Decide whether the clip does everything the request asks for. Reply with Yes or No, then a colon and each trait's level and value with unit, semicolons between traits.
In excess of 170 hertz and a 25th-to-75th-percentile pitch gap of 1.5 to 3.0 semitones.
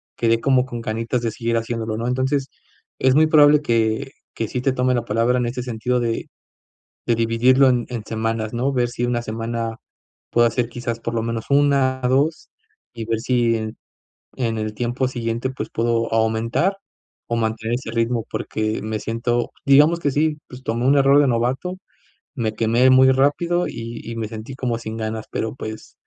No: low, 120 Hz; narrow, 2.4 semitones